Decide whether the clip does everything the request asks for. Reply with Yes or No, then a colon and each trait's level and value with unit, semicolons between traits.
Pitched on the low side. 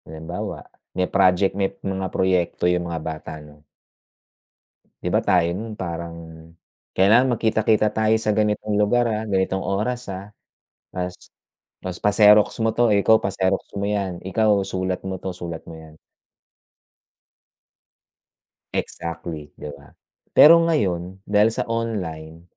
Yes: very low, 95 Hz